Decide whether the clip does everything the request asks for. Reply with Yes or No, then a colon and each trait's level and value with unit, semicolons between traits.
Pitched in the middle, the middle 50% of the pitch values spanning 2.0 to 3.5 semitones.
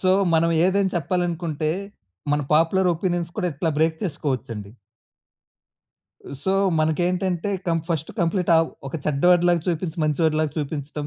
Yes: medium, 165 Hz; narrow, 2.5 semitones